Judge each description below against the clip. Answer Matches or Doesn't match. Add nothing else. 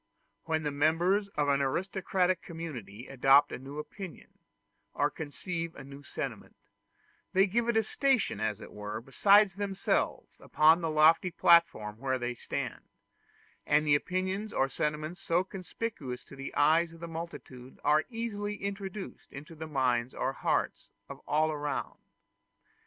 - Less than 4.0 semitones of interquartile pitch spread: Doesn't match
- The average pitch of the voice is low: Doesn't match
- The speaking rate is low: Doesn't match